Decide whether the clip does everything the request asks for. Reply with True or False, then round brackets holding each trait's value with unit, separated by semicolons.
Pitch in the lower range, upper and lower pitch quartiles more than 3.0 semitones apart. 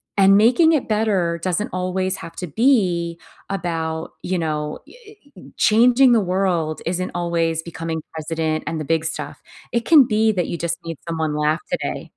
False (170 Hz; 4.0 semitones)